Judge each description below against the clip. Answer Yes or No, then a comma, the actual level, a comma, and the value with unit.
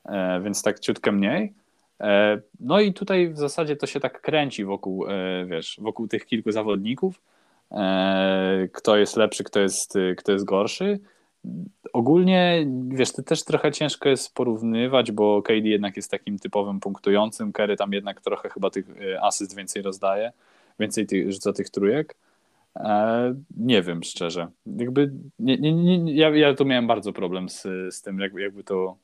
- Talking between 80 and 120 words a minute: No, average, 155 wpm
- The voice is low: Yes, low, 105 Hz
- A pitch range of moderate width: No, wide, 6.5 semitones